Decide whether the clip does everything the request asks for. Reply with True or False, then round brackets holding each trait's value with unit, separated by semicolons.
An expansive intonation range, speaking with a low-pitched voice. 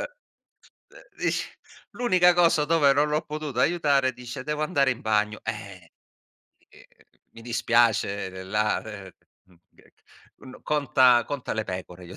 True (6.0 semitones; 130 Hz)